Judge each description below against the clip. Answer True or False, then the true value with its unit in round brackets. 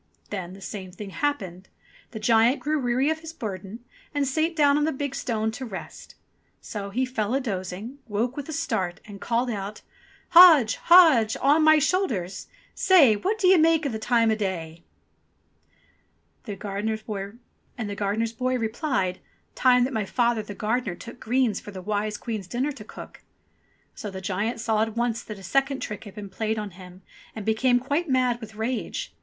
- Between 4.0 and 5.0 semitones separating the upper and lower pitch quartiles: True (4.7 semitones)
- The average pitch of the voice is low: False (225 Hz)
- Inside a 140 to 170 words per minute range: False (180 wpm)